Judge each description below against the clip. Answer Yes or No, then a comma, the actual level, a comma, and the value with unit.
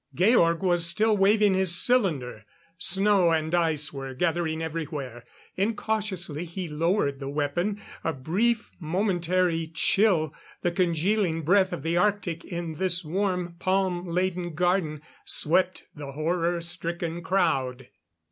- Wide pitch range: No, average, 3.1 semitones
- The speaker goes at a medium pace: No, slow, 125 wpm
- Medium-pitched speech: Yes, medium, 175 Hz